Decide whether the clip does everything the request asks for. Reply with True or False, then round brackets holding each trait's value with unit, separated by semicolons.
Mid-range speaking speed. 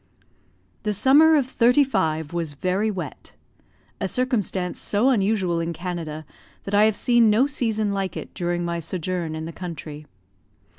True (150 wpm)